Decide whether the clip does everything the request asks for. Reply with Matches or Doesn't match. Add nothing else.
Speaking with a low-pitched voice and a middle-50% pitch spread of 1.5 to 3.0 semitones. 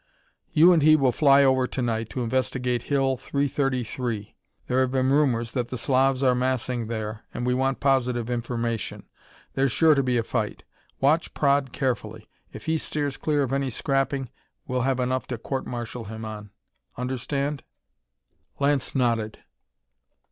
Matches